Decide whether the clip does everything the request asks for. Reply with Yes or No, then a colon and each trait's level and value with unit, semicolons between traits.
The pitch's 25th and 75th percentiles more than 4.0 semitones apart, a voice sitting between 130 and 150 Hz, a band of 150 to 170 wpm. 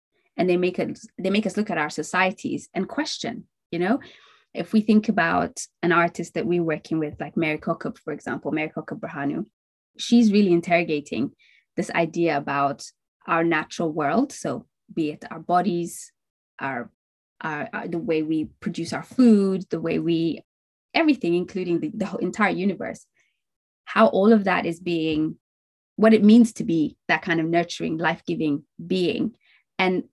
No: average, 5.0 semitones; medium, 175 Hz; average, 165 wpm